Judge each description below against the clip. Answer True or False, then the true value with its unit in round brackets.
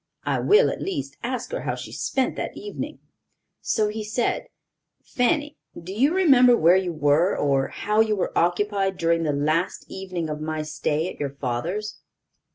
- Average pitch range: False (7.7 semitones)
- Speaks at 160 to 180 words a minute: True (170 wpm)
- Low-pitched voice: False (190 Hz)